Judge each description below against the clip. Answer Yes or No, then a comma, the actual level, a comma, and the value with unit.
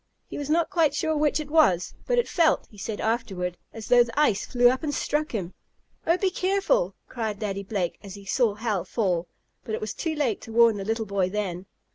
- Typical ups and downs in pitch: No, wide, 7.1 semitones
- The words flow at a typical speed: No, fast, 225 wpm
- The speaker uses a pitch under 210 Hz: No, high, 225 Hz